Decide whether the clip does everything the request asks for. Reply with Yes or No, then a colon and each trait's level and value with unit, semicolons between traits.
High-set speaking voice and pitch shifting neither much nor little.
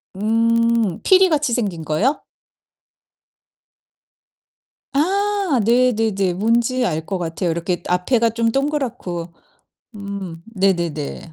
No: high, 220 Hz; wide, 6.1 semitones